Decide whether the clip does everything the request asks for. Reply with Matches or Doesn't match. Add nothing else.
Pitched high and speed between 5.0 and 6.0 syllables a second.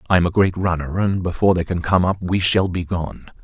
Doesn't match